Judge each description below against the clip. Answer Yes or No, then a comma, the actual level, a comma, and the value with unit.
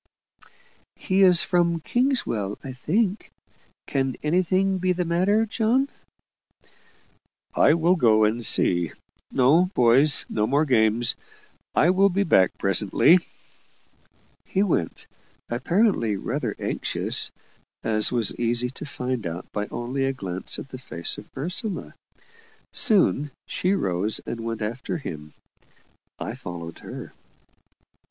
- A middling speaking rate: No, slow, 120 wpm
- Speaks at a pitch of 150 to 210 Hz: No, low, 135 Hz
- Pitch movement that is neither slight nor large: No, wide, 8.8 semitones